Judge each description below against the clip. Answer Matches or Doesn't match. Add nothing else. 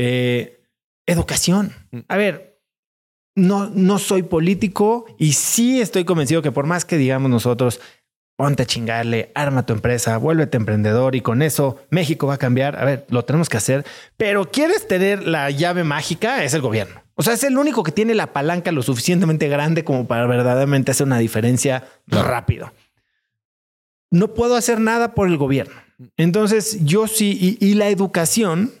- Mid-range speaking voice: Matches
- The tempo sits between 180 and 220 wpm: Doesn't match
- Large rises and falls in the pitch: Matches